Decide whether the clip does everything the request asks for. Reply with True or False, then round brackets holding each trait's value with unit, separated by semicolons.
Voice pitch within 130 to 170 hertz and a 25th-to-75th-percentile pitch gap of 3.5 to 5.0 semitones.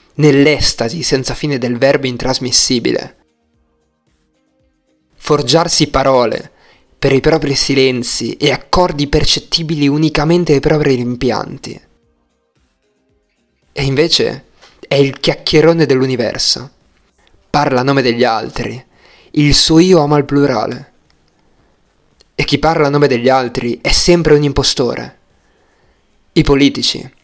False (140 Hz; 3.0 semitones)